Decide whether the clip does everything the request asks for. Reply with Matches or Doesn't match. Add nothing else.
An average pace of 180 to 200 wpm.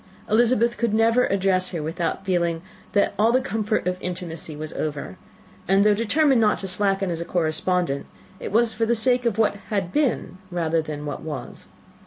Matches